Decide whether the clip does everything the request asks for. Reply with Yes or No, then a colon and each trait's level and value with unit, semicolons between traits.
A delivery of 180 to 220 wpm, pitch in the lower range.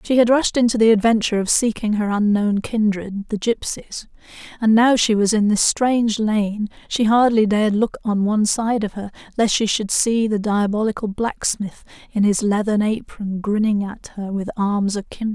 No: average, 185 wpm; high, 215 Hz